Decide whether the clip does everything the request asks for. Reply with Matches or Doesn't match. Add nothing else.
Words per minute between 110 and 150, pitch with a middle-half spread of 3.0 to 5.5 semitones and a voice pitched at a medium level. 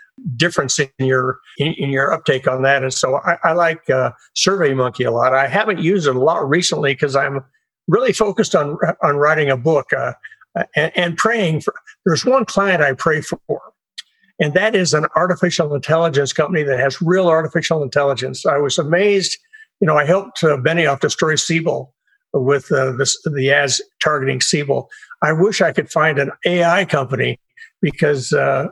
Doesn't match